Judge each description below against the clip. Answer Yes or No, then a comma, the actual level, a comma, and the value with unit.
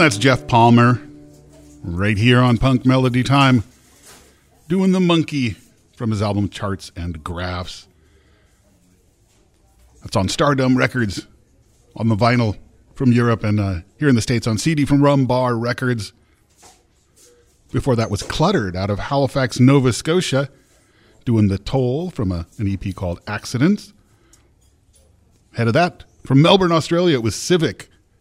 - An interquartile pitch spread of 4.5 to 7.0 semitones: Yes, average, 5.2 semitones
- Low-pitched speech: Yes, low, 115 Hz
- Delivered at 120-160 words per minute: Yes, average, 140 wpm